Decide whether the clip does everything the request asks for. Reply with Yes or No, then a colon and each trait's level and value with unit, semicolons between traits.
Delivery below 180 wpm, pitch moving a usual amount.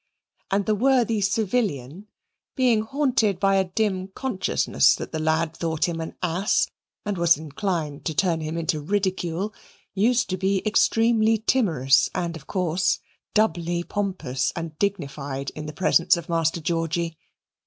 Yes: average, 145 wpm; average, 4.2 semitones